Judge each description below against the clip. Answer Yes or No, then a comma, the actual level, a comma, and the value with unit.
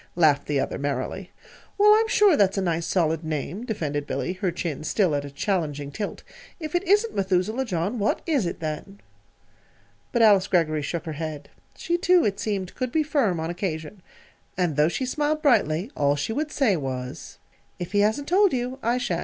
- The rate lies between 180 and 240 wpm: Yes, average, 195 wpm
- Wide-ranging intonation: Yes, wide, 8.2 semitones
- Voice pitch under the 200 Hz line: Yes, high, 190 Hz